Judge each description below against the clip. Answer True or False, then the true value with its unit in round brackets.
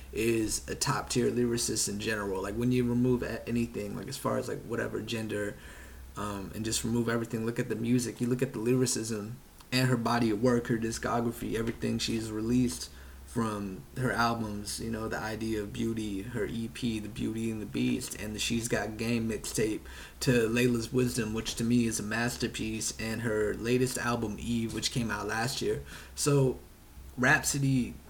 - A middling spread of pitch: False (1.9 semitones)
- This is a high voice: False (115 Hz)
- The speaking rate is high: False (185 wpm)